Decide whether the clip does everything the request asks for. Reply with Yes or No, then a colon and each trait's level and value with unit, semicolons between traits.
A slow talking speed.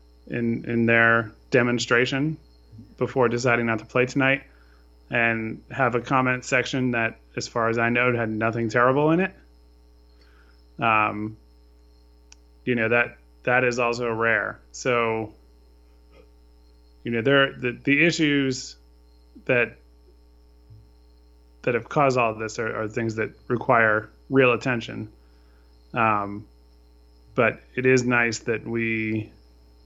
Yes: slow, 125 wpm